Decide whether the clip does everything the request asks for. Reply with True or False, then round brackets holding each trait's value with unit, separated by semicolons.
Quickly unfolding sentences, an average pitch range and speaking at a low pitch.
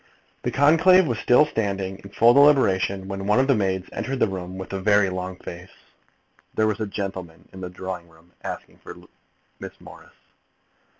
False (180 wpm; 3.9 semitones; 95 Hz)